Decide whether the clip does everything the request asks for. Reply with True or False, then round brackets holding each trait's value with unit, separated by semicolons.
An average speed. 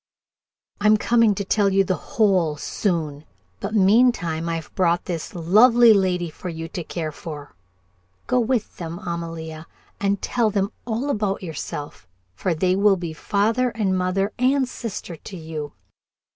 True (155 wpm)